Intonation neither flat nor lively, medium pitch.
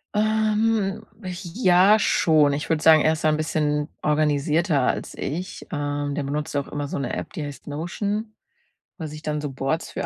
Yes: average, 4.2 semitones; medium, 155 Hz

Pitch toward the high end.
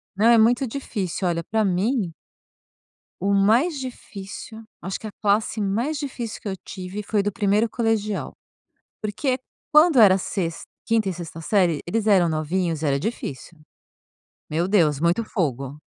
Yes: high, 200 Hz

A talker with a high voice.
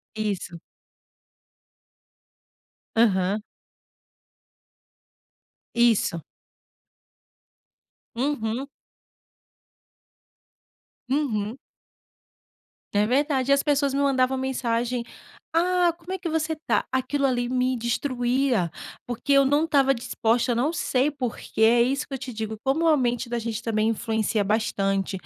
Yes: very high, 250 Hz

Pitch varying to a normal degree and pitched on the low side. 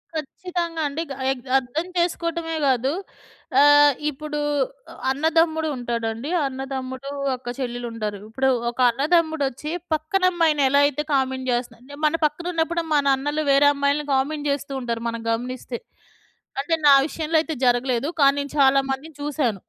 No: average, 3.4 semitones; very high, 280 Hz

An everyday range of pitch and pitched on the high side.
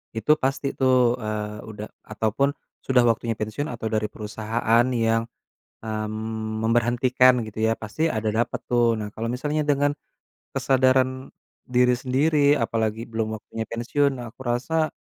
No: average, 3.1 semitones; low, 115 Hz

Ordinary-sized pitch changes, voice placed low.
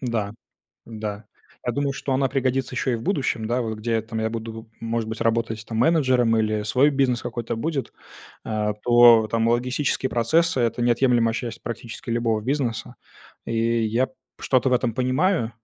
No: narrow, 2.3 semitones; low, 115 Hz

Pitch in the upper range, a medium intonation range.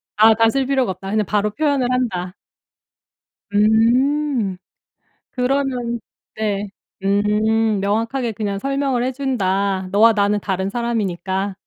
Yes: high, 220 Hz; average, 3.9 semitones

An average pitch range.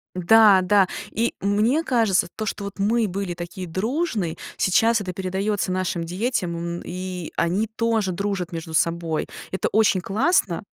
Yes: average, 3.6 semitones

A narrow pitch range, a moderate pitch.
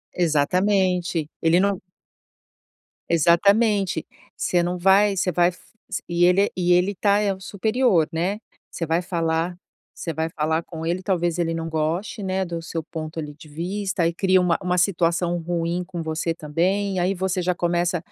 Yes: narrow, 2.3 semitones; medium, 175 Hz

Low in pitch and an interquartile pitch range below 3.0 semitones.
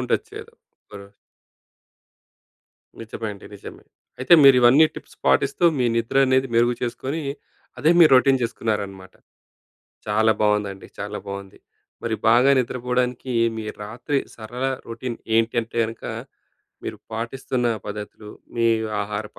No: low, 115 Hz; average, 3.3 semitones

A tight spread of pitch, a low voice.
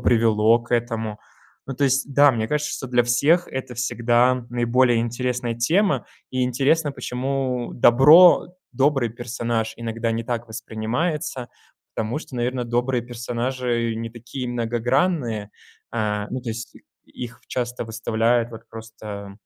Yes: narrow, 2.0 semitones; low, 120 Hz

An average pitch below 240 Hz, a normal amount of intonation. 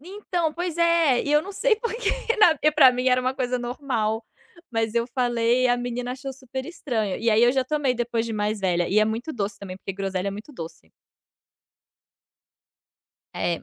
No: high, 245 Hz; average, 5.0 semitones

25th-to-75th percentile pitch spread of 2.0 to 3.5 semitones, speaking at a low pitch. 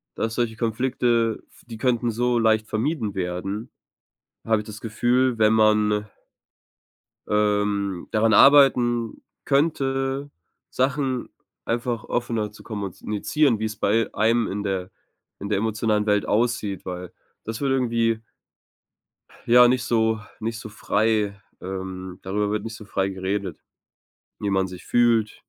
Yes: narrow, 2.6 semitones; low, 110 Hz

